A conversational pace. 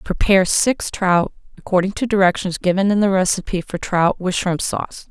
Yes: average, 175 wpm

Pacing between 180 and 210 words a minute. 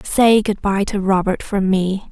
Yes: average, 200 wpm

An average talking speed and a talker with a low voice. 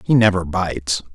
Yes: average, 160 wpm; very low, 90 Hz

